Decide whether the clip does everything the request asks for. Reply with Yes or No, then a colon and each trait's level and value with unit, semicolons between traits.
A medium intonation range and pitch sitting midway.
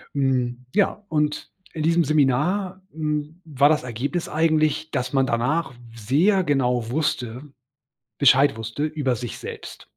Yes: average, 3.8 semitones; medium, 145 Hz